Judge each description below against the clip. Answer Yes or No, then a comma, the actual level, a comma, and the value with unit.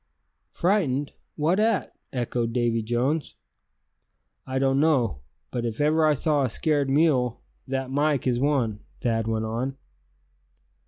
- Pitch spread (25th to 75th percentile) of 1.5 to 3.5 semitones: No, average, 3.9 semitones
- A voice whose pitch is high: No, low, 135 Hz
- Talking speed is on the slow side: Yes, slow, 130 wpm